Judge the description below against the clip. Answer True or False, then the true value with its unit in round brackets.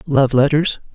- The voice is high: False (145 Hz)